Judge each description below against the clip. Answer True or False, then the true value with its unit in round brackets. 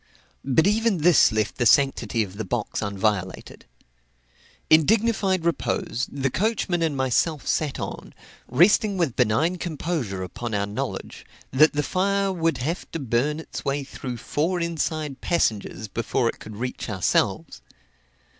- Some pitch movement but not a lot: False (6.6 semitones)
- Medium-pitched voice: True (145 Hz)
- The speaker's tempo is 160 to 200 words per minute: False (145 wpm)